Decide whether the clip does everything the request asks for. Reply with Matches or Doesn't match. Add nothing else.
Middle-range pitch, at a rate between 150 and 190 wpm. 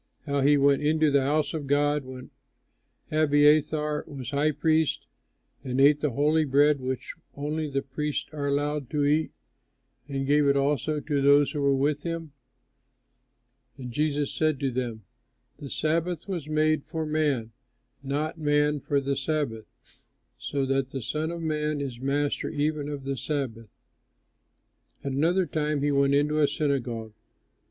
Matches